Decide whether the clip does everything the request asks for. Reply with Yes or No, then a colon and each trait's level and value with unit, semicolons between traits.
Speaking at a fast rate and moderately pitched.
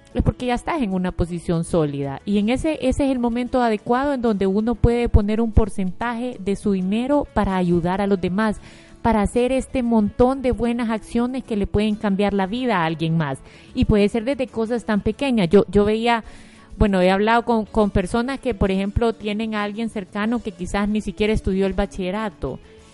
No: fast, 200 wpm; high, 215 Hz